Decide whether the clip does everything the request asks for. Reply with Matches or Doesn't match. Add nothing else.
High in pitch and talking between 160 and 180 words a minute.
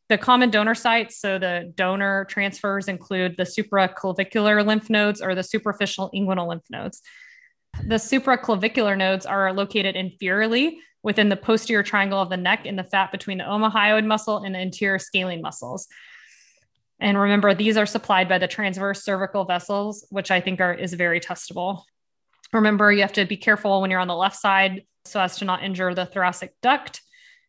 Matches